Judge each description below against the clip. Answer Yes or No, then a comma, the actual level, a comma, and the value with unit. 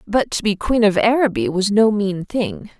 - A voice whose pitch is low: No, high, 210 Hz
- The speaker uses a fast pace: Yes, fast, 215 wpm